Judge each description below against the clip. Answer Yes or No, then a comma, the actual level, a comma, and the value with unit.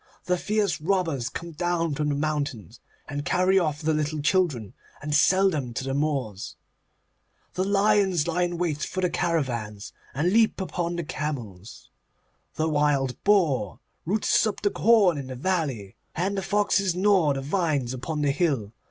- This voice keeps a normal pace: Yes, average, 165 wpm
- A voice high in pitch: No, medium, 155 Hz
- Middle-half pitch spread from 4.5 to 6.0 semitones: Yes, average, 4.9 semitones